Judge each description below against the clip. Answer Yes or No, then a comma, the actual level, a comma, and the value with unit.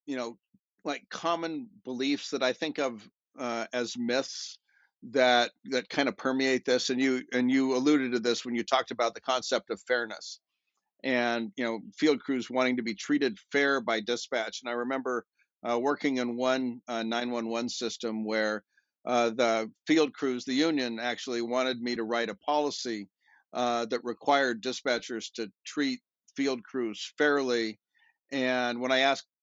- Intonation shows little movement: Yes, narrow, 2.1 semitones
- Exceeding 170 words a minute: No, average, 165 wpm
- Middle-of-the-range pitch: No, low, 125 Hz